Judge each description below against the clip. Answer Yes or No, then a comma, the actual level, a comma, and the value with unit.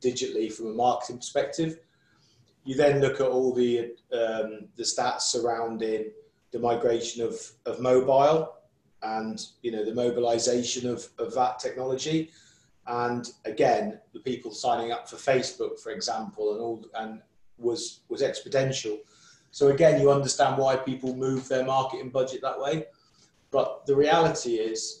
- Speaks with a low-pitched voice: Yes, low, 125 Hz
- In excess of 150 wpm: No, average, 145 wpm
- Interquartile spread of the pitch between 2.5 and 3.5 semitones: Yes, average, 3.2 semitones